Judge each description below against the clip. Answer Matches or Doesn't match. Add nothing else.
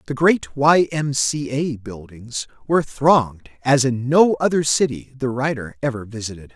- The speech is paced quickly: Doesn't match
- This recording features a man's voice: Matches